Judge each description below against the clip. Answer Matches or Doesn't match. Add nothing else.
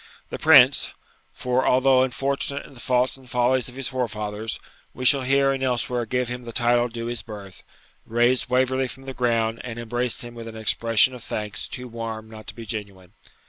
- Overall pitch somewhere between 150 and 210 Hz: Doesn't match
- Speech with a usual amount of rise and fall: Doesn't match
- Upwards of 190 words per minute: Matches